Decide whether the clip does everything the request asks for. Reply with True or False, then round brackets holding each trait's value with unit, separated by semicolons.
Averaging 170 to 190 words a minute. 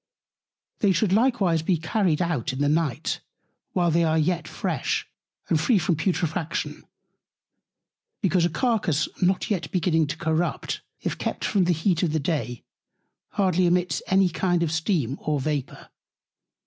False (150 wpm)